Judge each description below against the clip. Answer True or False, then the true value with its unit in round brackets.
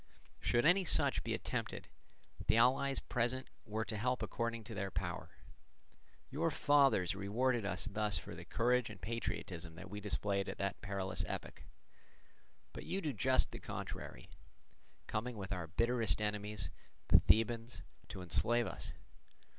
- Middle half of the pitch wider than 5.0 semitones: False (4.0 semitones)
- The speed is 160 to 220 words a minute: False (145 wpm)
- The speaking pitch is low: True (110 Hz)